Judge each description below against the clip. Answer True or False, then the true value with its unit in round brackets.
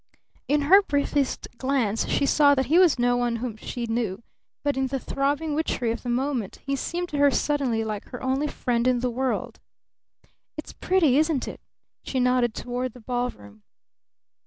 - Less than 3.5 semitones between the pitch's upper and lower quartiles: True (3.0 semitones)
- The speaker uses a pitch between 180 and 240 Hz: False (255 Hz)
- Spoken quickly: False (180 wpm)